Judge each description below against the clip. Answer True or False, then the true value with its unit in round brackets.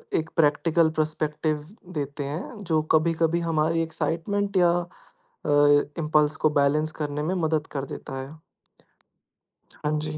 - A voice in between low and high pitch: True (155 Hz)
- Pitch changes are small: True (1.6 semitones)